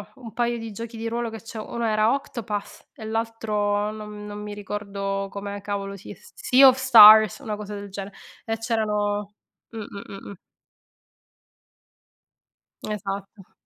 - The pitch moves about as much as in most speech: No, narrow, 1.9 semitones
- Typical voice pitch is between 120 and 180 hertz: No, high, 210 Hz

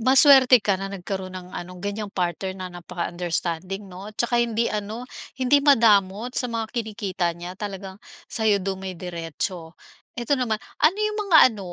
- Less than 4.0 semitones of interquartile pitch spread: No, average, 4.3 semitones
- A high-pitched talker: Yes, high, 200 Hz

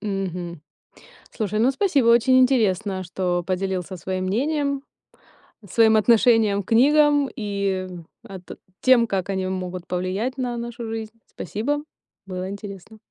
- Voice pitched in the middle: No, high, 210 Hz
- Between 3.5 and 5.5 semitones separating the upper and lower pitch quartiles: Yes, average, 4.4 semitones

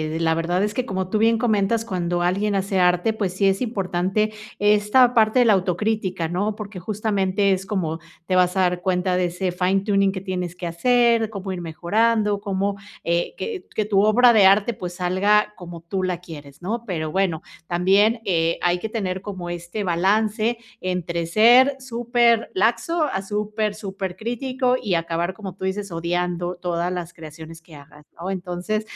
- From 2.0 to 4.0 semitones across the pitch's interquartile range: Yes, average, 3.3 semitones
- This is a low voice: No, high, 190 Hz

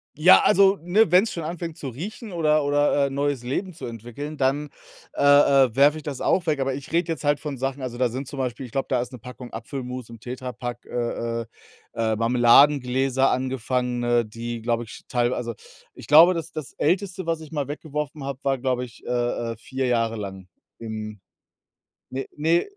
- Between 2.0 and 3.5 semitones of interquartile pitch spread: No, average, 3.9 semitones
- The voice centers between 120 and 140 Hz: Yes, low, 135 Hz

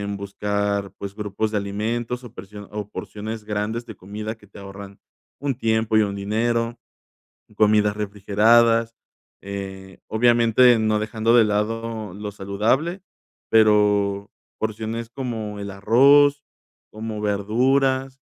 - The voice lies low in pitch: Yes, low, 110 Hz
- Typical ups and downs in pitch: No, narrow, 2.2 semitones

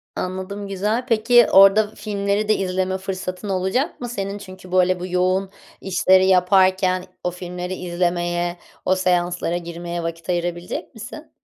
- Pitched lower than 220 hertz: Yes, medium, 185 Hz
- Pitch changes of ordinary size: No, narrow, 1.9 semitones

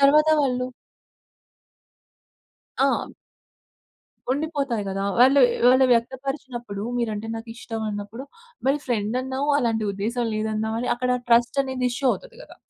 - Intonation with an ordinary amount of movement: Yes, average, 3.2 semitones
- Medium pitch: No, high, 245 Hz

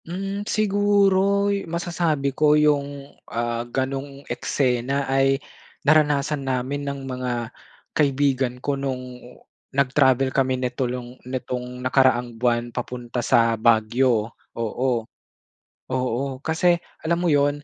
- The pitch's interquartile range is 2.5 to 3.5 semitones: Yes, average, 2.8 semitones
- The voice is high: No, low, 135 Hz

